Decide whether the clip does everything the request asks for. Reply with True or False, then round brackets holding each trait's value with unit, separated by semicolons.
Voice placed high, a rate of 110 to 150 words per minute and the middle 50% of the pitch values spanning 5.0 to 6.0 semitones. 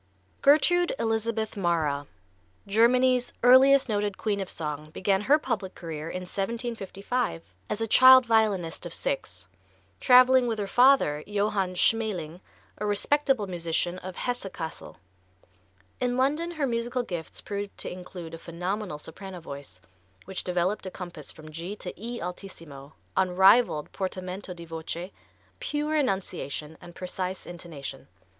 True (195 Hz; 135 wpm; 5.5 semitones)